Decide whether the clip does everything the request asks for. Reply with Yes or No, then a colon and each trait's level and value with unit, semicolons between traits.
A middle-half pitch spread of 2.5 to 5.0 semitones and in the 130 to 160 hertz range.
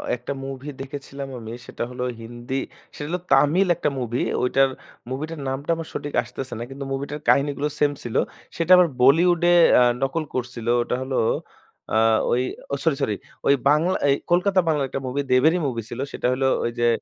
Yes: average, 3.3 semitones; low, 135 Hz